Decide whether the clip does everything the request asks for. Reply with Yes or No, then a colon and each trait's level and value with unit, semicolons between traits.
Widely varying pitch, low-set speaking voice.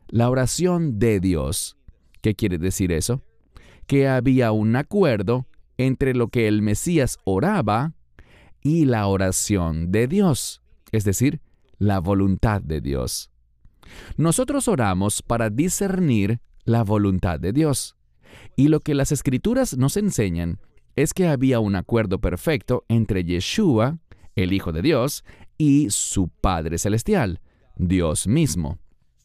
Yes: wide, 6.7 semitones; low, 110 Hz